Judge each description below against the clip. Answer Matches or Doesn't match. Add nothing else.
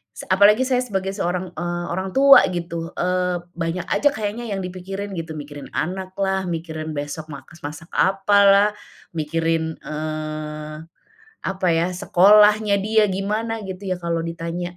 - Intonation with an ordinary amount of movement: Matches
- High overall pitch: Doesn't match